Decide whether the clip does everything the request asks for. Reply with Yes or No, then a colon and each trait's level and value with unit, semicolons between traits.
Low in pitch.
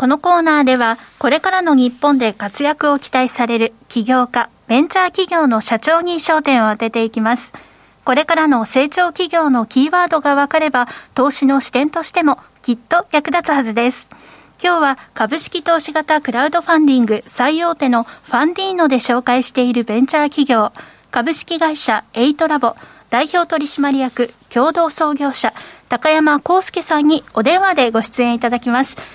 No: very high, 280 Hz